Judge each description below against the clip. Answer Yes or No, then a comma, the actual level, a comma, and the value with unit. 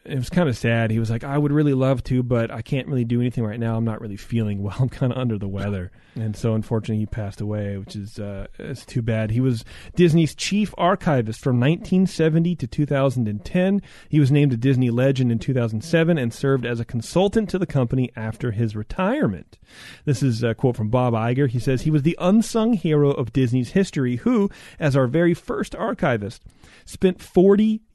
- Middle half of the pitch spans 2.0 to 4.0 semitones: No, average, 5.2 semitones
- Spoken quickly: Yes, fast, 210 wpm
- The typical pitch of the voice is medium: No, low, 130 Hz